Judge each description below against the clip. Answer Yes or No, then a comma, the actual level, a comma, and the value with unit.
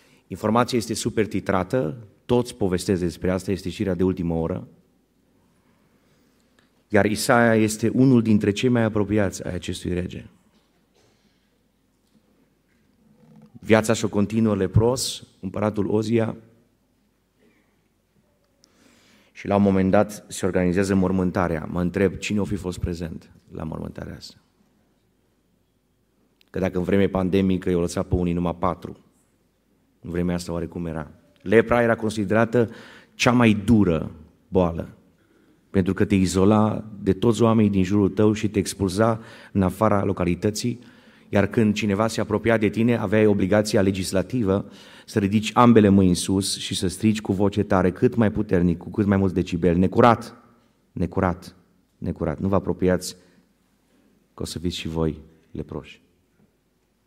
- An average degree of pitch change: Yes, average, 3.1 semitones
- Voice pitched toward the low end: Yes, low, 100 Hz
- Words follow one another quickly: No, average, 135 wpm